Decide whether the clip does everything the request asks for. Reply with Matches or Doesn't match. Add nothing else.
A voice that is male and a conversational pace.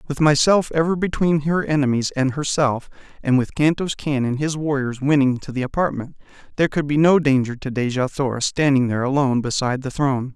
Matches